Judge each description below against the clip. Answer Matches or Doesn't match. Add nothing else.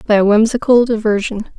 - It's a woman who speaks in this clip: Matches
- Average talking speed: Matches